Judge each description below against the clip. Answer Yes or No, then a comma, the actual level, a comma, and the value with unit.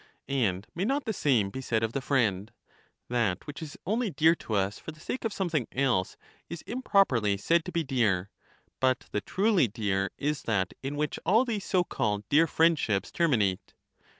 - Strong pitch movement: Yes, wide, 8.3 semitones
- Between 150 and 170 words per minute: No, average, 190 wpm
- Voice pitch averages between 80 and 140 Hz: Yes, low, 135 Hz